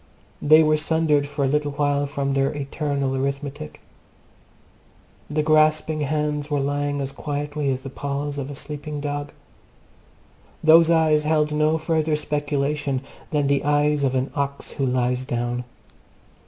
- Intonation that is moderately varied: No, narrow, 1.6 semitones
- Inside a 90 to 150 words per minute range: Yes, average, 145 wpm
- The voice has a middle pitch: Yes, medium, 145 Hz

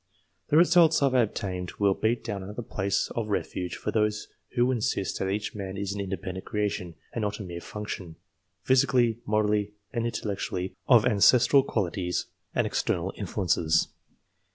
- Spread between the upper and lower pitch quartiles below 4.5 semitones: Yes, average, 3.6 semitones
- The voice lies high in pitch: No, low, 105 Hz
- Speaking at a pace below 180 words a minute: Yes, average, 160 wpm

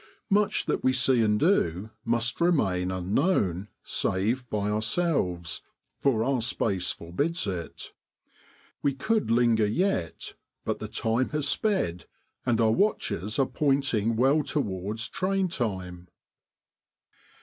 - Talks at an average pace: No, slow, 120 wpm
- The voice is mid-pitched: No, low, 115 Hz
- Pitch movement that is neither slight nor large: No, wide, 6.7 semitones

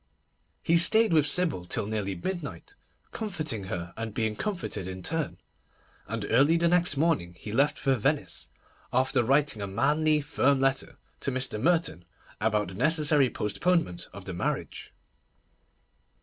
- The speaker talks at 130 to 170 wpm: Yes, average, 145 wpm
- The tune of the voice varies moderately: No, wide, 7.4 semitones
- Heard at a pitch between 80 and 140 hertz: Yes, low, 135 Hz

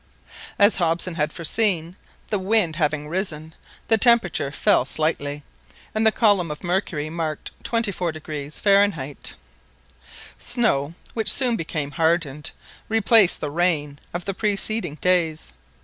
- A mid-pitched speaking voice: Yes, medium, 170 Hz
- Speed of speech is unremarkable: No, slow, 120 wpm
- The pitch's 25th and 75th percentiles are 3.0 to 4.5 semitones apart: No, average, 5.0 semitones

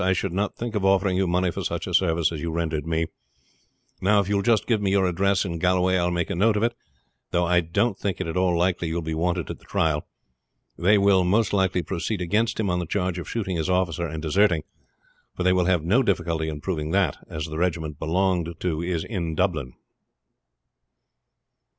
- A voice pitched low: Yes, very low, 90 Hz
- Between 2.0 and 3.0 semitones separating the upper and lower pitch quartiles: Yes, average, 2.7 semitones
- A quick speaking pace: Yes, fast, 230 wpm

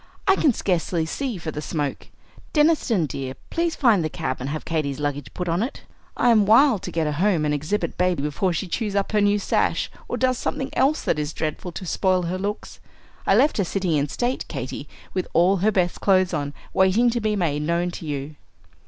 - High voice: No, medium, 180 Hz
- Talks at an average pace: No, fast, 215 wpm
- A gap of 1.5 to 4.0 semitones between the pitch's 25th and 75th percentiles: No, wide, 5.5 semitones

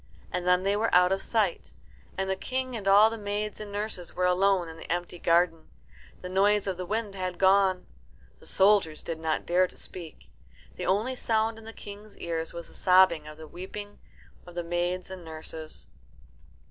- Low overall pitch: No, medium, 185 Hz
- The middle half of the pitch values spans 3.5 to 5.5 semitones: No, average, 2.9 semitones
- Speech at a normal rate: Yes, average, 190 wpm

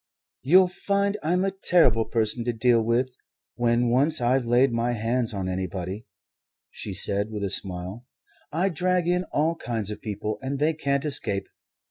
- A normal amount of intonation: No, wide, 6.6 semitones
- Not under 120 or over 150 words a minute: No, average, 165 wpm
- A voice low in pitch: Yes, low, 120 Hz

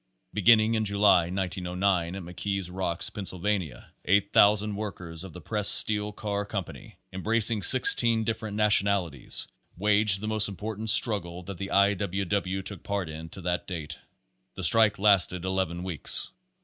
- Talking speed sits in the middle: Yes, average, 155 wpm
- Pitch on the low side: Yes, low, 100 Hz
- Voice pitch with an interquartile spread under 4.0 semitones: Yes, average, 2.7 semitones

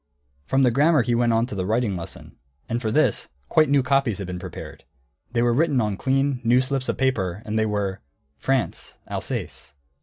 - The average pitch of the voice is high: No, low, 120 Hz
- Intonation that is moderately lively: Yes, average, 4.2 semitones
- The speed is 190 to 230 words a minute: Yes, average, 200 wpm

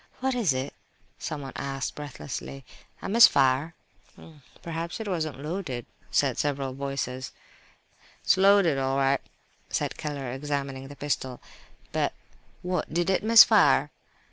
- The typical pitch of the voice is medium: Yes, medium, 145 Hz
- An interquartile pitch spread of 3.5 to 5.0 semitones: Yes, average, 4.2 semitones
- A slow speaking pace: Yes, slow, 120 wpm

